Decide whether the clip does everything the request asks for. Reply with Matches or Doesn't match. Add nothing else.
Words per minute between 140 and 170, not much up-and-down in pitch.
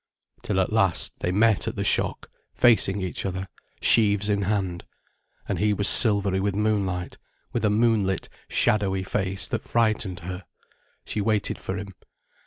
Matches